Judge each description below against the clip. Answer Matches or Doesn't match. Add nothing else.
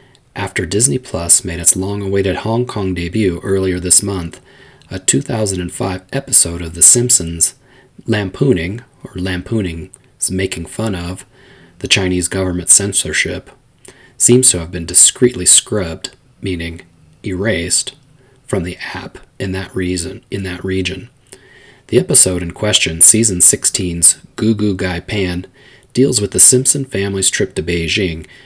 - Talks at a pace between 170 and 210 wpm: Doesn't match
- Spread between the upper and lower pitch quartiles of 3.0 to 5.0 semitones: Matches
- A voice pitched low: Matches